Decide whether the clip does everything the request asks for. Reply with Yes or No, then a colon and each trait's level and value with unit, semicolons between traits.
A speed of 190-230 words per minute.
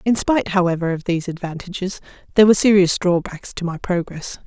No: average, 175 wpm